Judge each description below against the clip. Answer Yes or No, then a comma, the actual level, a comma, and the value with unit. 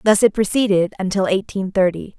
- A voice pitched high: Yes, high, 195 Hz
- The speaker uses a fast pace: No, average, 165 wpm